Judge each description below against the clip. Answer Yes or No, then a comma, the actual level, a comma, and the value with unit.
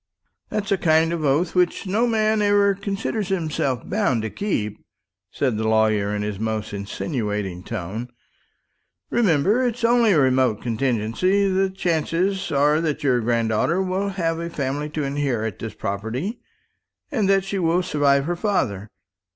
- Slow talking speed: No, average, 150 wpm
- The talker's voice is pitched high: No, medium, 155 Hz